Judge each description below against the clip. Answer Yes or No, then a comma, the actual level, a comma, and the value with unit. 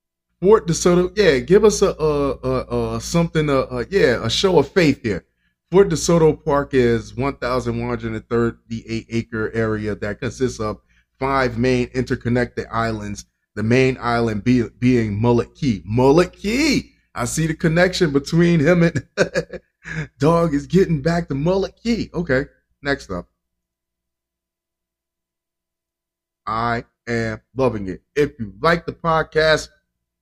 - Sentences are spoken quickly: No, slow, 135 wpm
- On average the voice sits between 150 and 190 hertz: No, low, 130 Hz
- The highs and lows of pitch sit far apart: Yes, wide, 6.4 semitones